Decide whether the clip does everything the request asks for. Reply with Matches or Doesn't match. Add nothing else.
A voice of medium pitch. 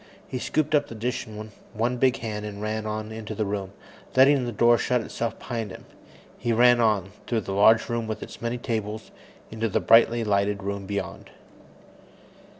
Doesn't match